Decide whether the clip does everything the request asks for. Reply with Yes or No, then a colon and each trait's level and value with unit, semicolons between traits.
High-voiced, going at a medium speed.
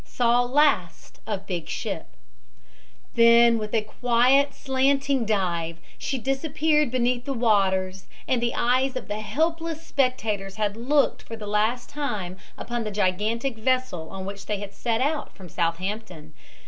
Yes: high, 230 Hz; average, 150 wpm